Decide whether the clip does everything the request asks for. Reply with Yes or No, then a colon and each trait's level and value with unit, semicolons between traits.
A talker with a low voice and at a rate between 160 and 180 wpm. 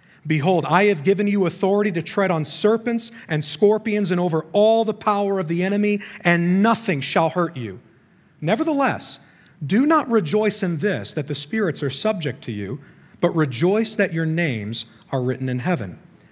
No: medium, 180 Hz; average, 175 wpm